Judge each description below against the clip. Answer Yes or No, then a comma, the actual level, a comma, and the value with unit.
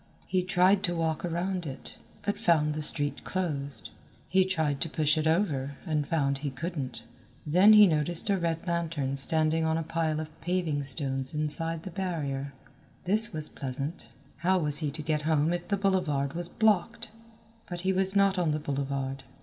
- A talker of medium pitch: Yes, medium, 160 Hz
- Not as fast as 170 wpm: No, average, 180 wpm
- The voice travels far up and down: No, average, 3.7 semitones